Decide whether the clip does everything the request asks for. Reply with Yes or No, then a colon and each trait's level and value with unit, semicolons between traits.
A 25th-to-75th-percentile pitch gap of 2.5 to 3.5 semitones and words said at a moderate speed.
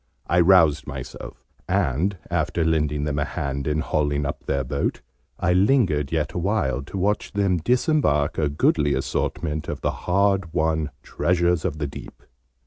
No: average, 4.0 semitones; average, 155 wpm